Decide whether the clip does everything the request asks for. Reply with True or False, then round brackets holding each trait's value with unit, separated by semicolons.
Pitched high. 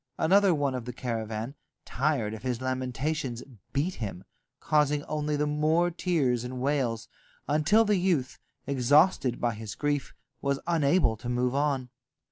False (140 Hz)